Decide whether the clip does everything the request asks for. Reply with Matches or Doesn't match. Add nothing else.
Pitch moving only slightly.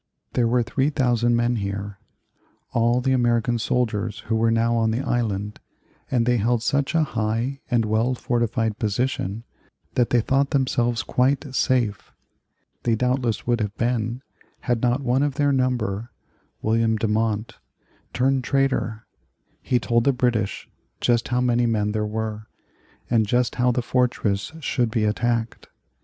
Matches